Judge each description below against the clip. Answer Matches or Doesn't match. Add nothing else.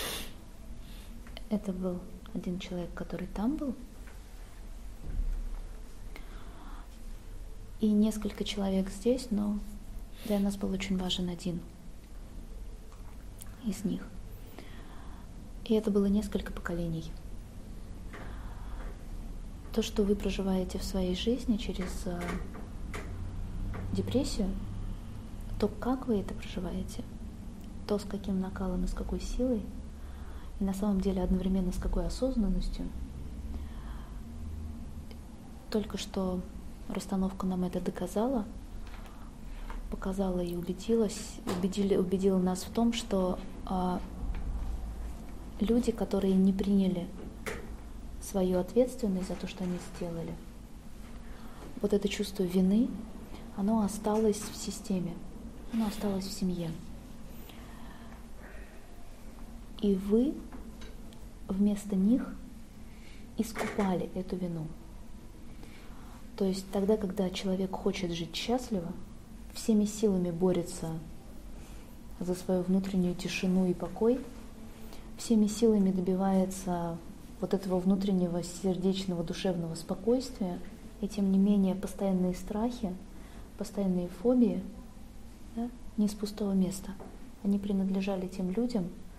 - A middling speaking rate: Doesn't match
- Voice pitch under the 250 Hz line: Matches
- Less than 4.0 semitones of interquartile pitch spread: Matches